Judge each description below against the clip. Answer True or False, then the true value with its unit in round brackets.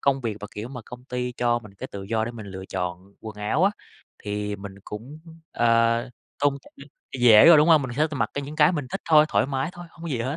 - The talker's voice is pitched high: False (120 Hz)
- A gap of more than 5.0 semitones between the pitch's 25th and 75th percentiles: True (5.4 semitones)